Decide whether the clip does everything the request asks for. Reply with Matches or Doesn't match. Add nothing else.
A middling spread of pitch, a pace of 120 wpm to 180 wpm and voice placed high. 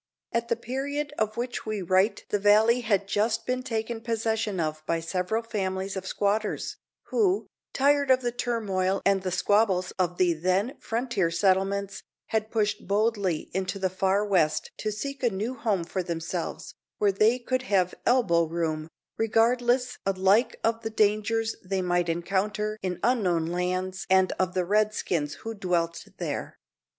Matches